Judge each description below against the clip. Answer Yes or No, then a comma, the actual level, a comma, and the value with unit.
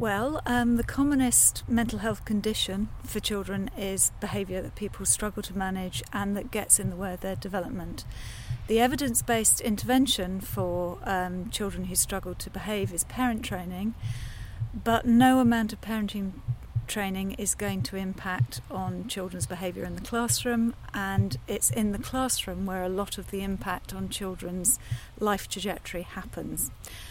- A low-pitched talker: No, high, 195 Hz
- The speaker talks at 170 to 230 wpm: No, average, 155 wpm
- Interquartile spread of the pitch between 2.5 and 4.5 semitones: Yes, average, 3.5 semitones